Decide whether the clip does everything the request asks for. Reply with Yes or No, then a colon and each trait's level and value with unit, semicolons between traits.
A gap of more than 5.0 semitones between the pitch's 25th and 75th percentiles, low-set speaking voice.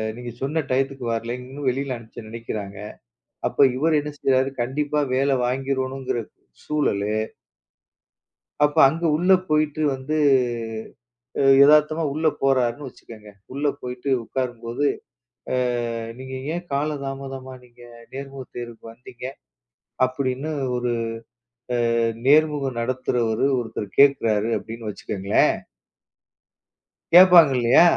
No: average, 3.2 semitones; low, 130 Hz